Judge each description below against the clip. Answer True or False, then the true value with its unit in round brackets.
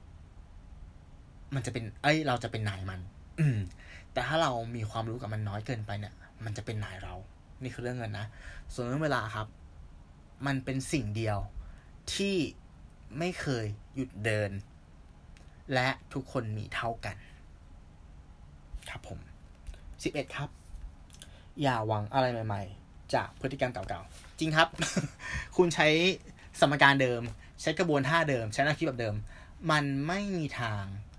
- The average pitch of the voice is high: False (105 Hz)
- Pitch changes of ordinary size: False (8.1 semitones)